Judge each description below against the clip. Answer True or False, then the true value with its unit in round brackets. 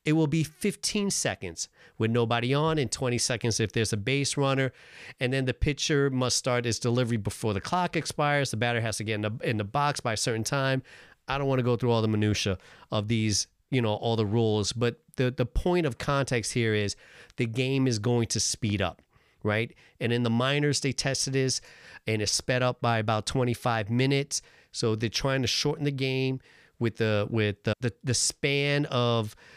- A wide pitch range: False (3.4 semitones)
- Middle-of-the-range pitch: False (120 Hz)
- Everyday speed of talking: False (210 wpm)